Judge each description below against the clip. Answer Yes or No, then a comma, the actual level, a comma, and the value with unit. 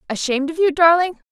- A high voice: Yes, very high, 315 Hz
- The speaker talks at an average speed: Yes, average, 180 wpm